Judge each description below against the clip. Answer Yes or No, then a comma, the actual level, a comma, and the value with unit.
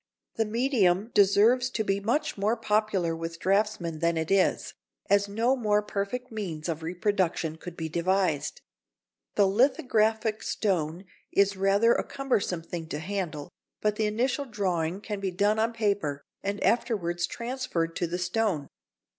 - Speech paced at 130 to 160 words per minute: Yes, average, 150 wpm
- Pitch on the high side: Yes, high, 200 Hz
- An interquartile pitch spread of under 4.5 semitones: Yes, average, 4.1 semitones